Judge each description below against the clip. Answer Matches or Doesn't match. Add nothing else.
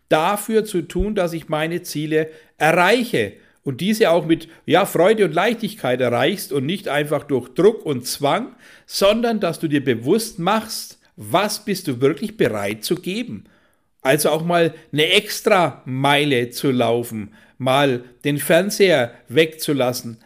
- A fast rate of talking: Doesn't match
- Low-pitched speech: Doesn't match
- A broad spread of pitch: Matches